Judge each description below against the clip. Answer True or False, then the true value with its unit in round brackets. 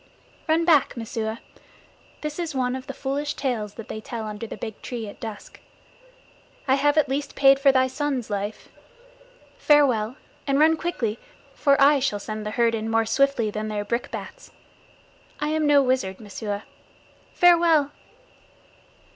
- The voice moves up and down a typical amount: True (4.9 semitones)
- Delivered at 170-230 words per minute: False (155 wpm)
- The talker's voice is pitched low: False (260 Hz)